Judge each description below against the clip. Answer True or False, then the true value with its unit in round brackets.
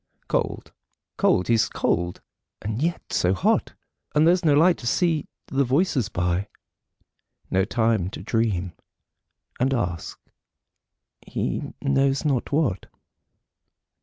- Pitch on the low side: True (120 Hz)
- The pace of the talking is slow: True (115 wpm)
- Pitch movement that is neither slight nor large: False (7.4 semitones)